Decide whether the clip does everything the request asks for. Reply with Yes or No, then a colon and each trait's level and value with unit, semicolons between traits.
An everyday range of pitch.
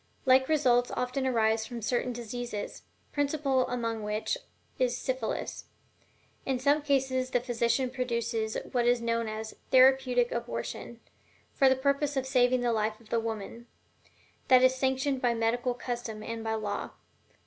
No: narrow, 2.3 semitones